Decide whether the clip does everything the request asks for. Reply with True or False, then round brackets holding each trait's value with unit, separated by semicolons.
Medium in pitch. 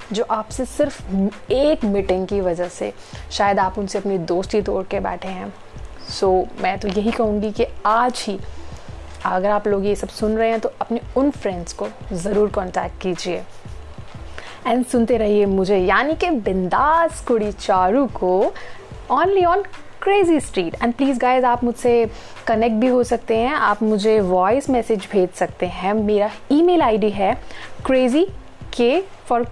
False (220 Hz)